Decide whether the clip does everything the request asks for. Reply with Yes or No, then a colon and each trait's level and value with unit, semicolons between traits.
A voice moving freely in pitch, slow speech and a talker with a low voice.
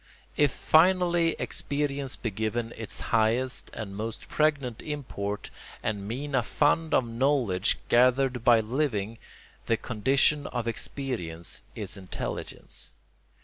No: average, 4.6 semitones; slow, 115 wpm; low, 120 Hz